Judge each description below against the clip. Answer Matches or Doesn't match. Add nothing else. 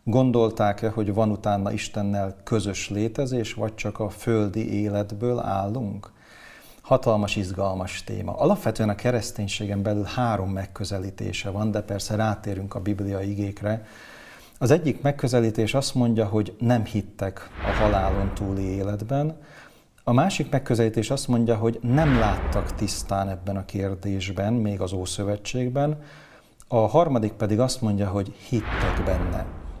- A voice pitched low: Matches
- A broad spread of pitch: Doesn't match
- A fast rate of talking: Doesn't match